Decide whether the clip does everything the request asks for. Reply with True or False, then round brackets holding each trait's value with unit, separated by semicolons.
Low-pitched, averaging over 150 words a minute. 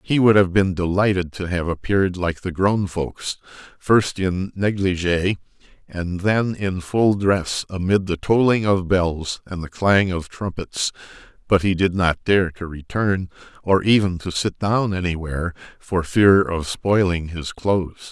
True (95 Hz; 160 wpm)